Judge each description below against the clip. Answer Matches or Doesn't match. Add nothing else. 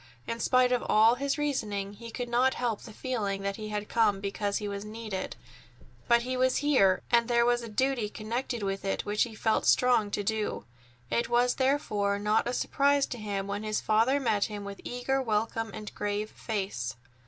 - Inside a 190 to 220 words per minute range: Matches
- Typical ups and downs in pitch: Matches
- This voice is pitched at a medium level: Doesn't match